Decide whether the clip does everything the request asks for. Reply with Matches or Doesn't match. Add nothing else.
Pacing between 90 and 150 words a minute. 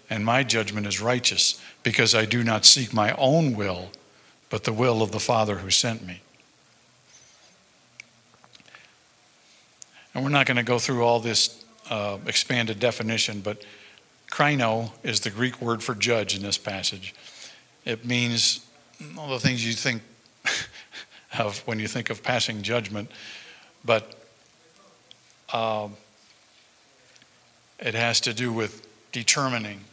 Matches